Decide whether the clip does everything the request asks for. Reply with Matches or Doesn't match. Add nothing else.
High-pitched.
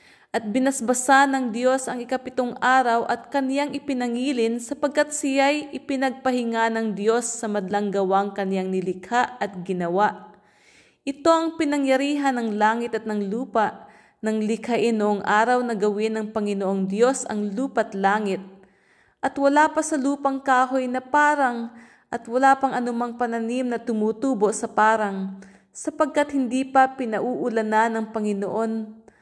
Matches